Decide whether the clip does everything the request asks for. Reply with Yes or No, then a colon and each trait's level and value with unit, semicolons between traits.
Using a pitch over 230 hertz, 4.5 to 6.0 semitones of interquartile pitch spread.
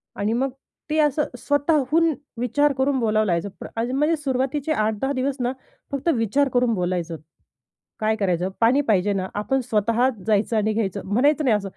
Yes: high, 240 Hz; average, 5.0 semitones